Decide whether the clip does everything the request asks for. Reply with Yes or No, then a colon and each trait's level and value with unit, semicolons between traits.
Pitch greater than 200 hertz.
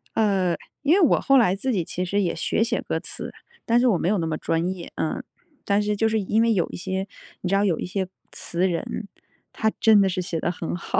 No: high, 195 Hz